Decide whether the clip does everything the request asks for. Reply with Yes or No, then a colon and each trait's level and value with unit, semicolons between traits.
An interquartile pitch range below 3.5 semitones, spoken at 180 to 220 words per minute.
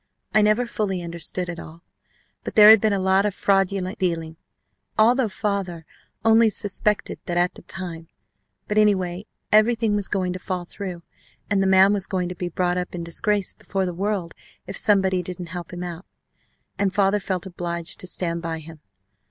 Yes: narrow, 2.6 semitones; average, 185 wpm